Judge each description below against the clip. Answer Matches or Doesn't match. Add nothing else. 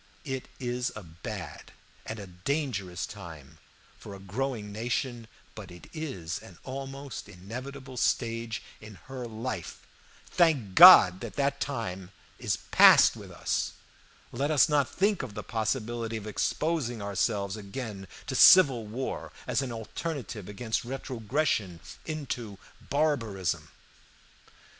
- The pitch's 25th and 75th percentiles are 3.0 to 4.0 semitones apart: Doesn't match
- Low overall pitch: Matches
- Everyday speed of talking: Doesn't match